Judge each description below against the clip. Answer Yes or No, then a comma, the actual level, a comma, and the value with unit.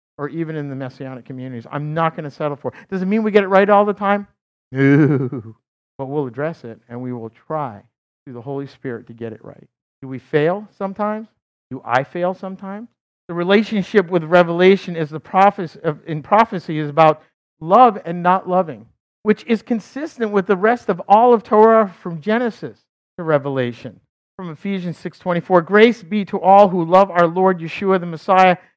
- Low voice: No, medium, 175 Hz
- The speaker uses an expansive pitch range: Yes, wide, 6.1 semitones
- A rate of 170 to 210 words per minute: Yes, average, 190 wpm